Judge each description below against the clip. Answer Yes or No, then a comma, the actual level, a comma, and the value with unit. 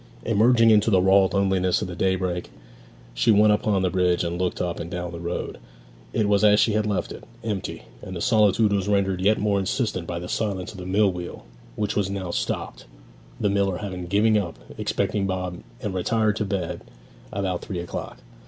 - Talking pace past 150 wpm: Yes, average, 200 wpm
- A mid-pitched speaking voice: No, very low, 95 Hz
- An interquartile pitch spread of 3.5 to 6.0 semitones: No, narrow, 2.5 semitones